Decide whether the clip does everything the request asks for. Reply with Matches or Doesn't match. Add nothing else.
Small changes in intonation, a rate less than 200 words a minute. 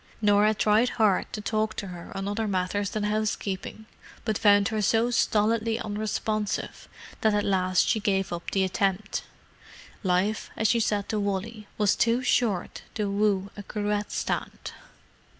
Matches